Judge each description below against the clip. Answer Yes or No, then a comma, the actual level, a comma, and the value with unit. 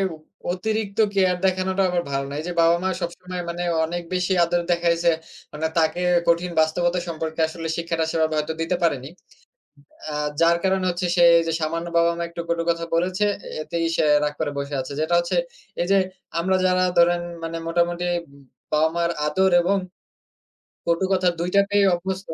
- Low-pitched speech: No, medium, 170 Hz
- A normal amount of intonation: No, narrow, 1.7 semitones